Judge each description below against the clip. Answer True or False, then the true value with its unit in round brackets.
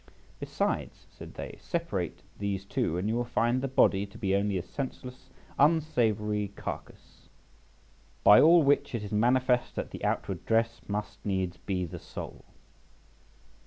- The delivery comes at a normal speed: True (150 wpm)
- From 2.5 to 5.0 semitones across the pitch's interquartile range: True (4.4 semitones)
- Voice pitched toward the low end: True (105 Hz)